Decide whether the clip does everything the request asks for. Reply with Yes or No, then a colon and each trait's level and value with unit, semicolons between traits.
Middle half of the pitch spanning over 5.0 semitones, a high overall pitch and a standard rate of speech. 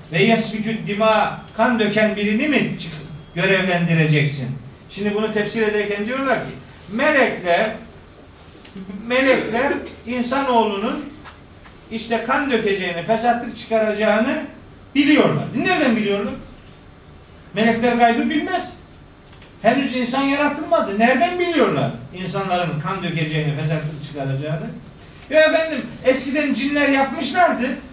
No: wide, 5.5 semitones; high, 220 Hz; slow, 90 wpm